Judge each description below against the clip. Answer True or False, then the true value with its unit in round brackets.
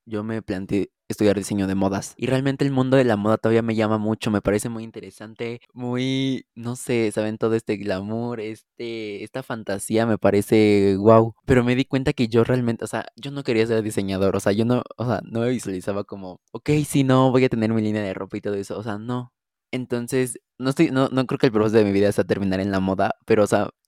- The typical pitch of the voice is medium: False (110 Hz)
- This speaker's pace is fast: True (240 wpm)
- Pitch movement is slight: False (3.3 semitones)